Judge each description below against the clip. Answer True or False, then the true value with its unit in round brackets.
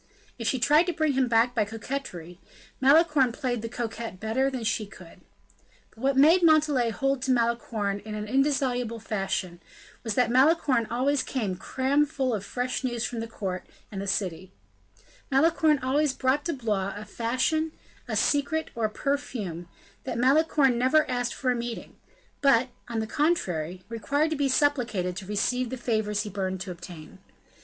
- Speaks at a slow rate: False (170 wpm)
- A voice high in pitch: True (245 Hz)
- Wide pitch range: False (4.6 semitones)